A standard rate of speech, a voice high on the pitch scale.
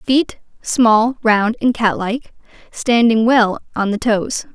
No: slow, 120 wpm; high, 230 Hz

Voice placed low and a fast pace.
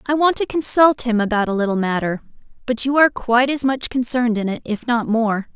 No: high, 240 Hz; fast, 225 wpm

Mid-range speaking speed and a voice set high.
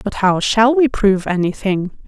Yes: average, 175 wpm; high, 210 Hz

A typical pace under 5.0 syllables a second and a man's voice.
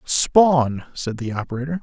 Yes: 4.3 syllables/s; male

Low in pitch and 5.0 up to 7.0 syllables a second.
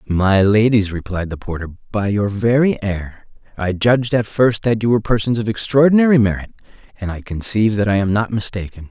Yes: low, 105 Hz; 5.5 syllables/s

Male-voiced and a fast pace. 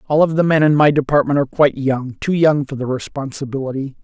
Yes: male; fast, 210 wpm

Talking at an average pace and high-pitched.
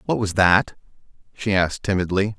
No: average, 150 wpm; very low, 95 Hz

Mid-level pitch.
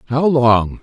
No: low, 130 Hz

